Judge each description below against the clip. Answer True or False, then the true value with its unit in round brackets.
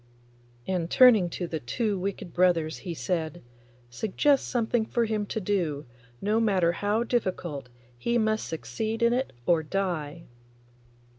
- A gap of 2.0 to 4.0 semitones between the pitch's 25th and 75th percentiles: False (4.8 semitones)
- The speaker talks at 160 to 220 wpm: False (140 wpm)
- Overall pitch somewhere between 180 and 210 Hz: True (190 Hz)